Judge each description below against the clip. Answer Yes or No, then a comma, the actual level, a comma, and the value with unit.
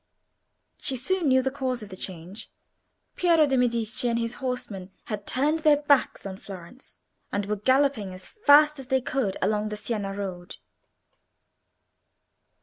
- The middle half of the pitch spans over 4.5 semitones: Yes, average, 5.2 semitones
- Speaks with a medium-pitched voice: No, high, 245 Hz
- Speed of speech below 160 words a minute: Yes, average, 150 wpm